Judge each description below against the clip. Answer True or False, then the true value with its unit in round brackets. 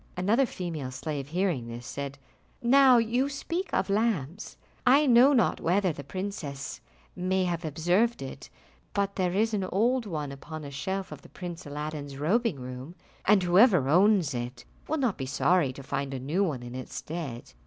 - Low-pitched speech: False (175 Hz)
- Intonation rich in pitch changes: True (6.9 semitones)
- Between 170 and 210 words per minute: True (175 wpm)